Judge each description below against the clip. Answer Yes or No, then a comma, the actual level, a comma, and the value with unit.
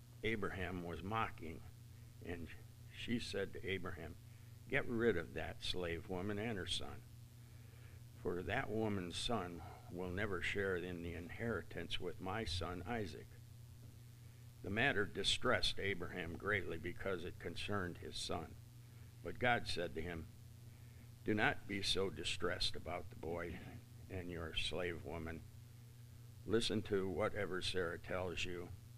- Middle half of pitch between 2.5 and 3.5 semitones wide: No, average, 4.3 semitones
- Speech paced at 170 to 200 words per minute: No, slow, 135 wpm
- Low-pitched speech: Yes, low, 110 Hz